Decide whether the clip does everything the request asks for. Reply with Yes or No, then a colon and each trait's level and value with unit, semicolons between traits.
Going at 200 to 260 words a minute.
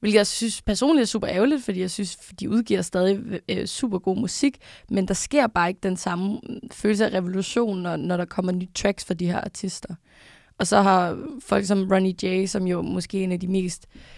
Yes: average, 220 wpm